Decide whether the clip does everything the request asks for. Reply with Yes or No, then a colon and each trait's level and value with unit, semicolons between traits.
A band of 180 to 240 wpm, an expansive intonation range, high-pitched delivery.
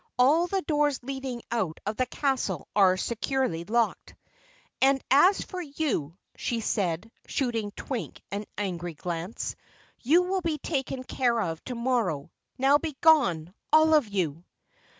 No: average, 140 wpm; wide, 7.2 semitones; high, 245 Hz